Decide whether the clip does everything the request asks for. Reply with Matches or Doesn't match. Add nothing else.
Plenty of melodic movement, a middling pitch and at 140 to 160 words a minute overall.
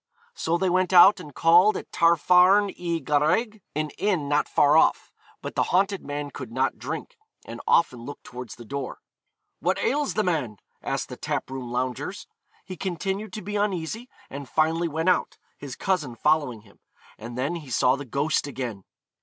Doesn't match